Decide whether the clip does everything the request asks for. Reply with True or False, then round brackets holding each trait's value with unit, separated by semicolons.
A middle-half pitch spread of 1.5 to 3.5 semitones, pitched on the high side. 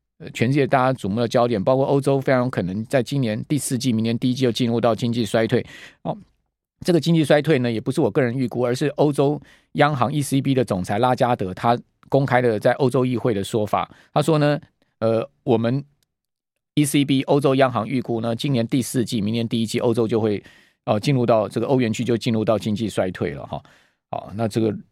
False (3.1 semitones; 125 Hz)